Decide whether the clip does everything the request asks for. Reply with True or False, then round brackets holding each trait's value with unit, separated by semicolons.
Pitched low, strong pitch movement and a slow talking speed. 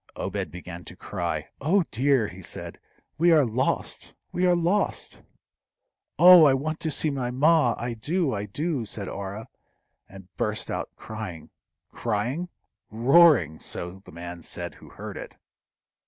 False (120 Hz; 8.5 semitones; 150 wpm)